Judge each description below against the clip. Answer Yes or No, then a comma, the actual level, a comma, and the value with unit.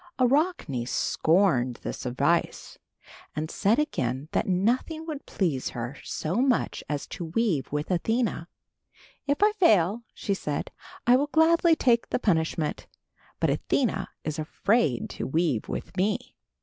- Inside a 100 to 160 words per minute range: Yes, slow, 135 wpm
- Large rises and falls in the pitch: Yes, wide, 8.7 semitones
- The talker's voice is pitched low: No, high, 190 Hz